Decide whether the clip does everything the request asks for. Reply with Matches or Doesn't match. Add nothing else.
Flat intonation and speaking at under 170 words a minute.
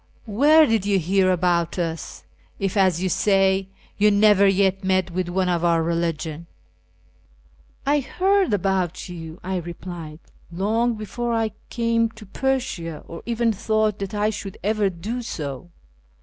Doesn't match